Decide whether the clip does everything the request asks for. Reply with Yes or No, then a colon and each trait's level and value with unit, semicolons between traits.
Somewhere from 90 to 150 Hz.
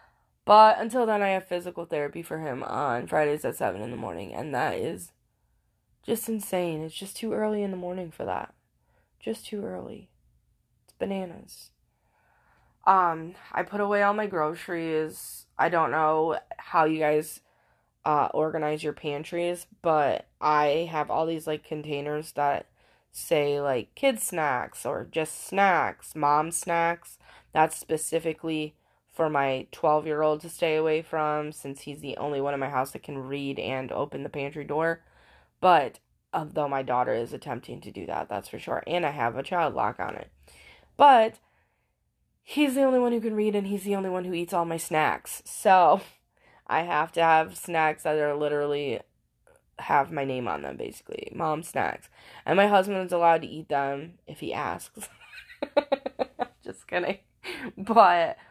No: medium, 160 Hz